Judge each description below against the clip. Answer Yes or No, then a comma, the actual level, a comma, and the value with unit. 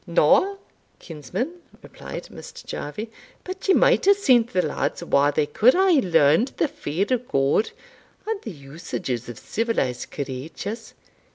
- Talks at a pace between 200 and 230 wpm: No, average, 145 wpm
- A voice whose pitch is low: No, high, 195 Hz